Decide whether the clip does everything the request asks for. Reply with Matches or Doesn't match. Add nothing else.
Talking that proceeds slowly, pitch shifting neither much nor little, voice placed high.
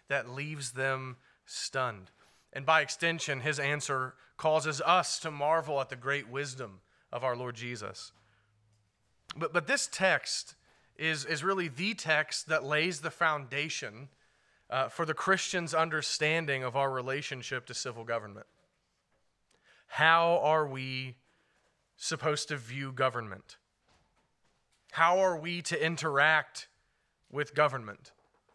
Doesn't match